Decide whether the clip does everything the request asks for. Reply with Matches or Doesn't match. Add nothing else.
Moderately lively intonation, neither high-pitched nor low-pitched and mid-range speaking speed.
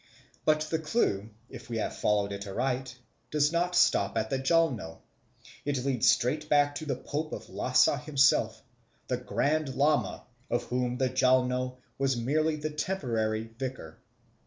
Doesn't match